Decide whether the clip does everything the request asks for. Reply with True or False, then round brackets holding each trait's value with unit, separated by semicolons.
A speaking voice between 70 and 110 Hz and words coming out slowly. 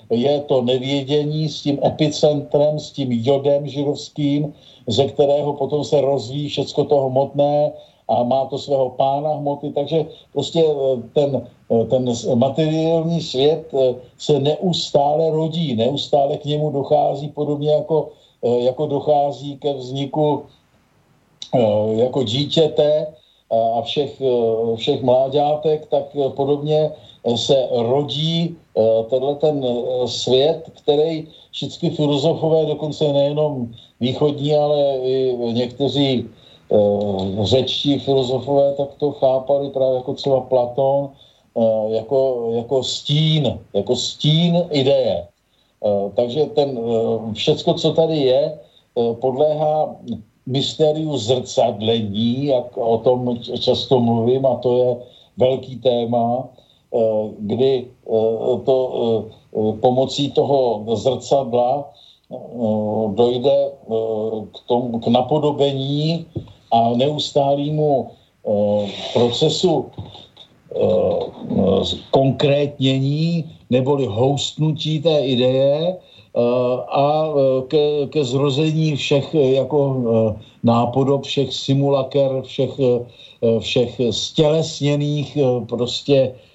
False (140 Hz; 90 wpm)